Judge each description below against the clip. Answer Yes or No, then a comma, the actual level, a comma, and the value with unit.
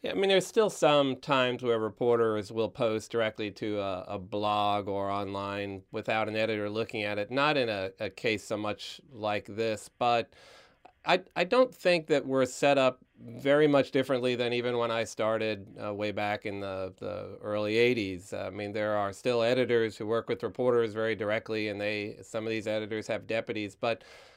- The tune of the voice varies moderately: Yes, average, 3.0 semitones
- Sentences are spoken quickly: No, average, 195 wpm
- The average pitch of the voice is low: Yes, low, 110 Hz